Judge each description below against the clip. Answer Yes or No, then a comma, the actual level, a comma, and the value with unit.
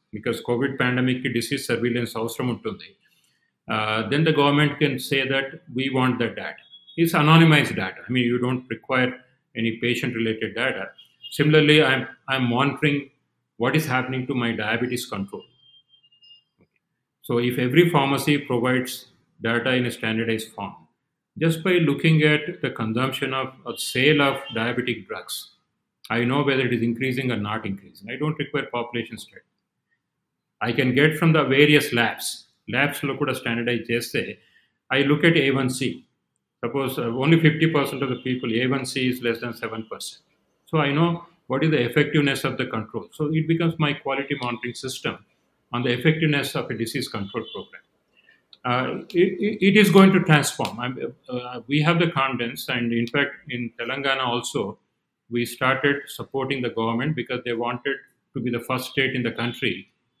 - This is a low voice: Yes, low, 130 Hz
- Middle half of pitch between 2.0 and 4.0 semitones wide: Yes, average, 3.4 semitones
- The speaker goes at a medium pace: No, fast, 165 wpm